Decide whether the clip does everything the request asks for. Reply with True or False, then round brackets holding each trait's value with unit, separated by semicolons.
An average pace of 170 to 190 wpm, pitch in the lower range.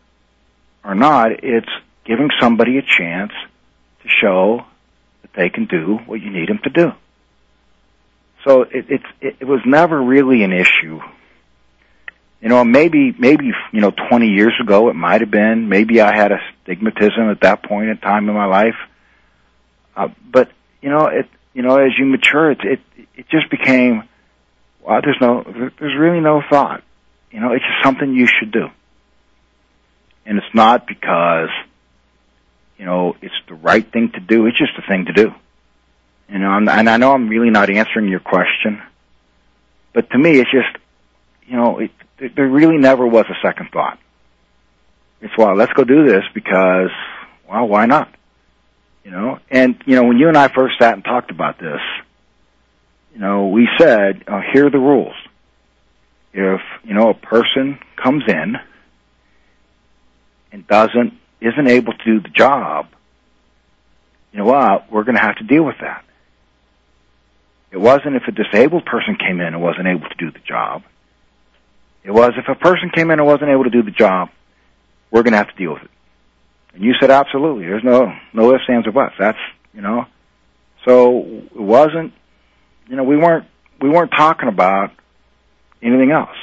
True (175 wpm; 110 Hz)